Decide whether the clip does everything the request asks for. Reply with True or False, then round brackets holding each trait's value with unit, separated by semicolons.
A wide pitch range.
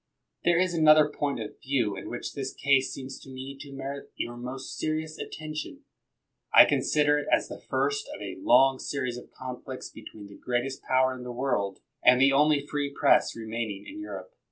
False (3.0 semitones)